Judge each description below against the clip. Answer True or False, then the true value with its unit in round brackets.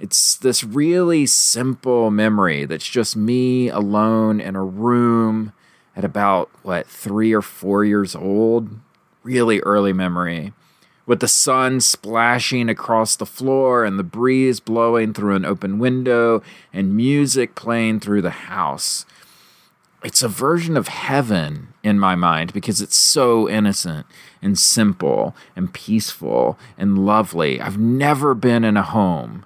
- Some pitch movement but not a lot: True (3.5 semitones)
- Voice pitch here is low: True (110 Hz)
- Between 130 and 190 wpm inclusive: True (140 wpm)